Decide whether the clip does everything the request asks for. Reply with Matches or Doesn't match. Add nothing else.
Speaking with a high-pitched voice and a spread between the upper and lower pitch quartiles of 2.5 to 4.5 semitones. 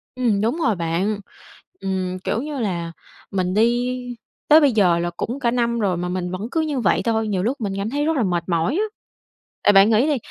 Doesn't match